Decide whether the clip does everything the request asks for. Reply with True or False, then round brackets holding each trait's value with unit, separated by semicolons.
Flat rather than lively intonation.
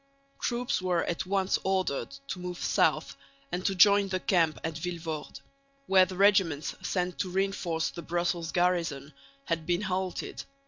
True (2.3 semitones)